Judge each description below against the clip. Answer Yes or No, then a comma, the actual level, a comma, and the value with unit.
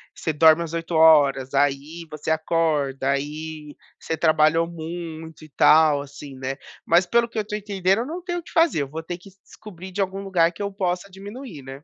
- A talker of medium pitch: Yes, medium, 165 Hz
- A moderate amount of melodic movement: Yes, average, 4.1 semitones